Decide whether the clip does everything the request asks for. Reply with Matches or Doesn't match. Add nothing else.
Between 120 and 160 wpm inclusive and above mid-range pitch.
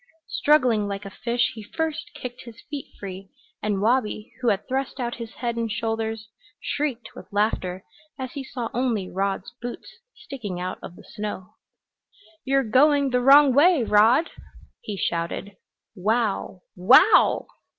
Matches